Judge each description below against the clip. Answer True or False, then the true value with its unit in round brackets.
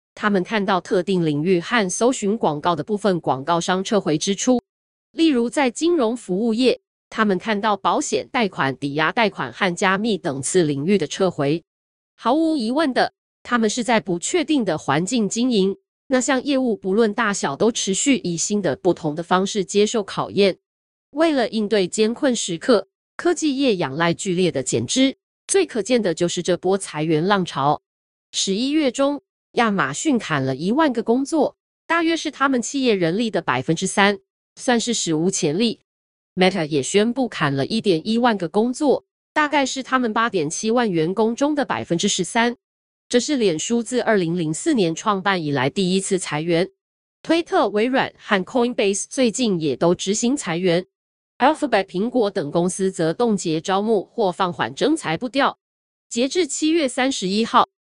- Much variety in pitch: True (5.9 semitones)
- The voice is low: False (210 Hz)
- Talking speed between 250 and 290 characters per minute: True (275 characters per minute)